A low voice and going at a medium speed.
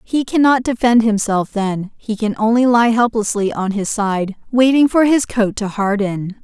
No: high, 225 Hz; average, 175 wpm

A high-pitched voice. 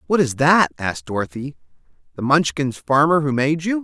No: medium, 140 Hz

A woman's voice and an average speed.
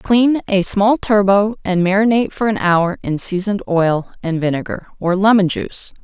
Yes: female; average, 170 wpm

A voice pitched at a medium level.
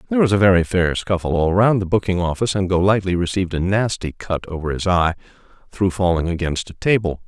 No: very low, 95 Hz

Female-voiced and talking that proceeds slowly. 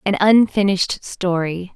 Yes: female; slow, 105 wpm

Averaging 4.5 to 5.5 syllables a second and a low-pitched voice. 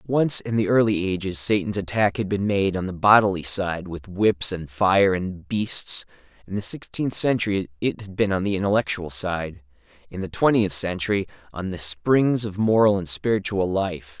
Yes: 4.7 syllables/s; very low, 95 Hz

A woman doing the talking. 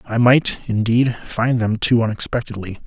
No: male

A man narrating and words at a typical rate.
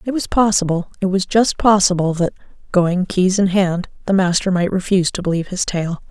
No: female; average, 195 wpm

